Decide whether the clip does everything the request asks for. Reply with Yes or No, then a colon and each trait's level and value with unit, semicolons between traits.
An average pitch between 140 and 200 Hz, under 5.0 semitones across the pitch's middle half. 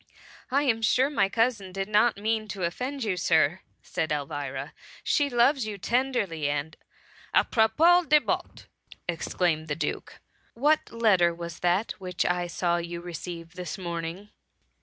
No: medium, 185 Hz; average, 5.3 semitones